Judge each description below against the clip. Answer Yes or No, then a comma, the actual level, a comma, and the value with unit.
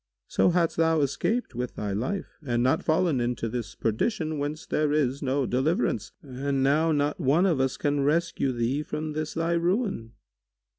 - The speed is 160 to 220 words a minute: Yes, average, 170 wpm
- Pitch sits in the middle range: Yes, medium, 145 Hz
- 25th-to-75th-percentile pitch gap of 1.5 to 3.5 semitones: No, average, 4.0 semitones